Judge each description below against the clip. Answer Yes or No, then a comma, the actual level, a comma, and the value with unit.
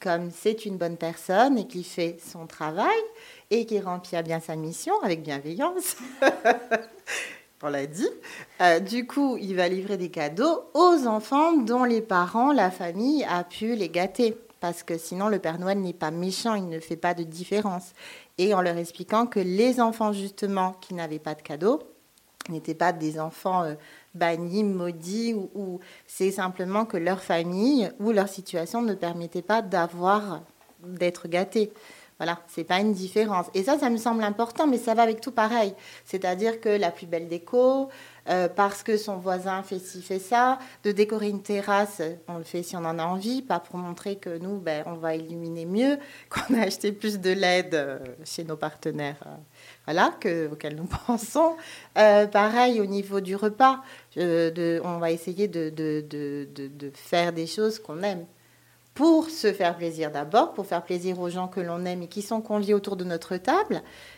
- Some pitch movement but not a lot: Yes, average, 4.3 semitones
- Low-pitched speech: No, medium, 185 Hz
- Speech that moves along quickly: No, average, 190 wpm